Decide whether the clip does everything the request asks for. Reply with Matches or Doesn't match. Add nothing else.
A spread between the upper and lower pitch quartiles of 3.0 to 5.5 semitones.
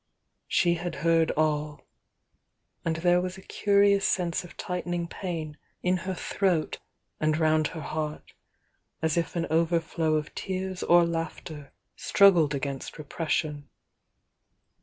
Doesn't match